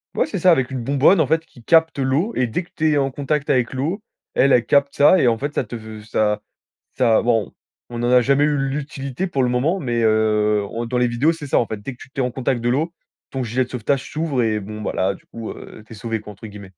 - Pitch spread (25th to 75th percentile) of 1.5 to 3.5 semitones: No, average, 4.1 semitones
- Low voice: Yes, low, 125 Hz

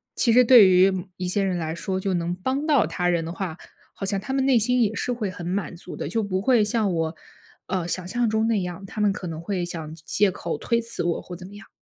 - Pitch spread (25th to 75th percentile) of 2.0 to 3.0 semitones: No, average, 4.2 semitones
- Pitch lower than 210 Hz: Yes, high, 195 Hz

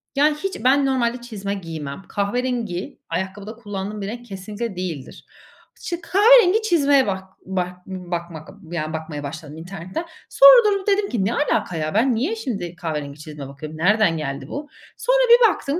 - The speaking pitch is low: No, high, 200 Hz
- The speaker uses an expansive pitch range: Yes, wide, 8.8 semitones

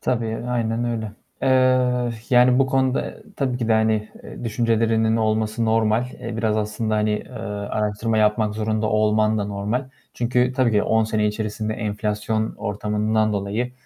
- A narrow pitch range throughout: Yes, narrow, 1.9 semitones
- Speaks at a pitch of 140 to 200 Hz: No, low, 110 Hz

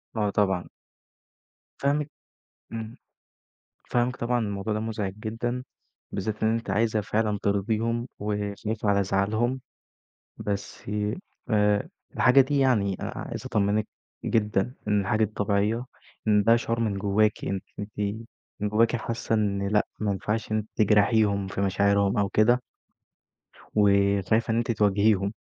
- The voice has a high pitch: No, low, 105 Hz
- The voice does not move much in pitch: Yes, narrow, 2.1 semitones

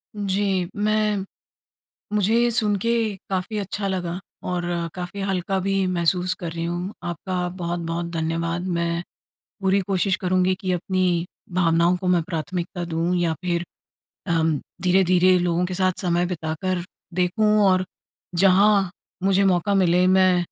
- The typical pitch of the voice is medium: Yes, medium, 180 Hz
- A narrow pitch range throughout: Yes, narrow, 2.0 semitones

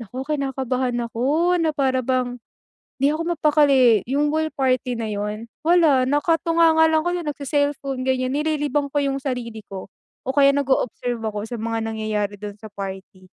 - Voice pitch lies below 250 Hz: No, very high, 265 Hz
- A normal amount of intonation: Yes, average, 4.4 semitones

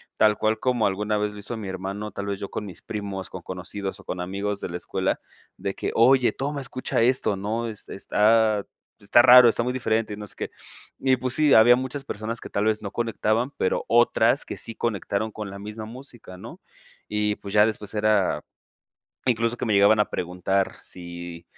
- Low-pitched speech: Yes, low, 105 Hz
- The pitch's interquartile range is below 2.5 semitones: No, average, 2.8 semitones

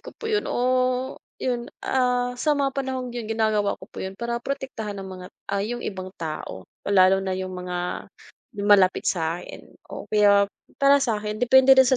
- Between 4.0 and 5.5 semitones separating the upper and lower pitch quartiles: Yes, average, 5.0 semitones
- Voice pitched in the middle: No, high, 220 Hz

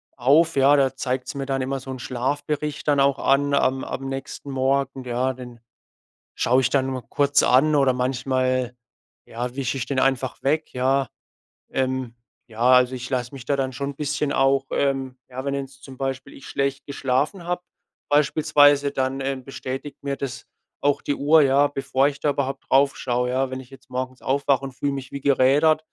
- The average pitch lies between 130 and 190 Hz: Yes, low, 135 Hz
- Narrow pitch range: Yes, narrow, 1.4 semitones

